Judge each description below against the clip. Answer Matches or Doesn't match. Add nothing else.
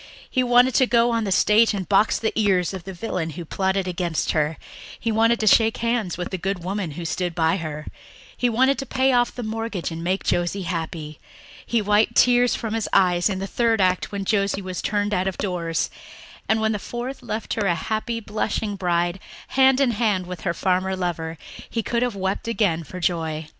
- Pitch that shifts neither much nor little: Matches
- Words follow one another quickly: Matches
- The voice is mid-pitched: Doesn't match